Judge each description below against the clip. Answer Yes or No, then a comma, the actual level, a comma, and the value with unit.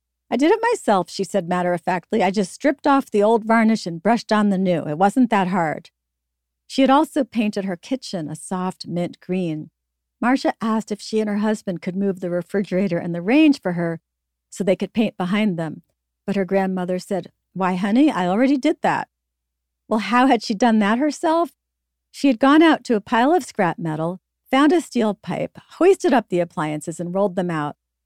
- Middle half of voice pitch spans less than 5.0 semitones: No, wide, 5.5 semitones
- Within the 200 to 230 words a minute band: Yes, fast, 205 wpm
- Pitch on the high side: Yes, high, 200 Hz